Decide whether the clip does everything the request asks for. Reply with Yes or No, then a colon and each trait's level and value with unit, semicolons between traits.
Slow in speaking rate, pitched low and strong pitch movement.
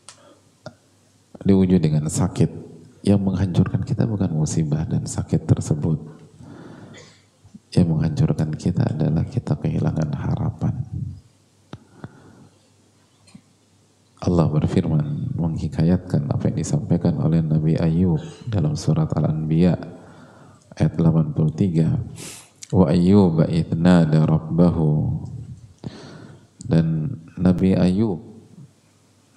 Yes: slow, 75 wpm; very low, 90 Hz; wide, 6.6 semitones